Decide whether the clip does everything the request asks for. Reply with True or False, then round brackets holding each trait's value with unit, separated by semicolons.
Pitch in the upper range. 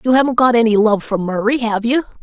True (230 Hz)